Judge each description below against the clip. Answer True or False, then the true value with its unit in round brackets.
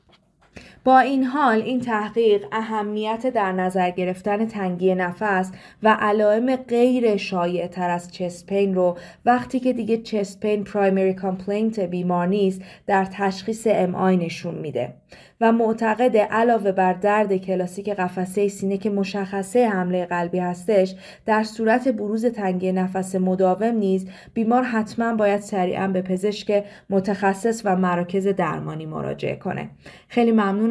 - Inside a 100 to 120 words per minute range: False (130 wpm)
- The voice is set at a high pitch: True (200 Hz)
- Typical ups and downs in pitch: True (3.0 semitones)